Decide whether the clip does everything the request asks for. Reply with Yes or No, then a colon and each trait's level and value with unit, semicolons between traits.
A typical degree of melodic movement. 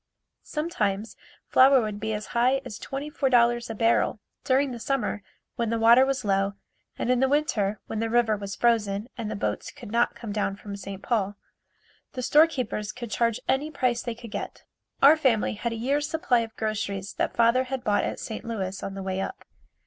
Yes: average, 3.8 semitones